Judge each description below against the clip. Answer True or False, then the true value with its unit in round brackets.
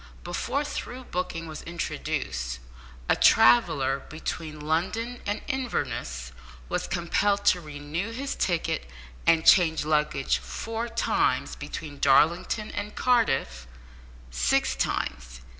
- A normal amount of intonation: False (6.8 semitones)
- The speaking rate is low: True (110 wpm)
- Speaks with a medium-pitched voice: True (165 Hz)